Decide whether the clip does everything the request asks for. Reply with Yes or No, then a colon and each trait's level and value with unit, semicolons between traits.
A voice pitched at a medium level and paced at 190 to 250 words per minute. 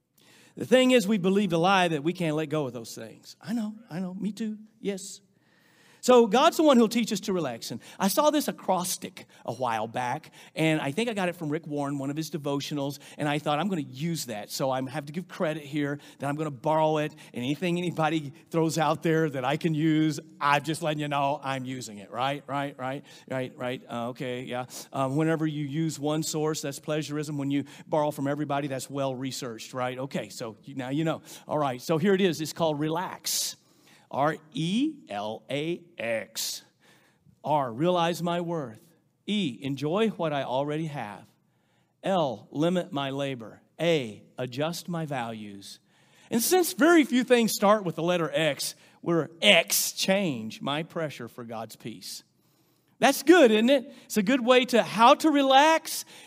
Yes: medium, 155 Hz; average, 195 wpm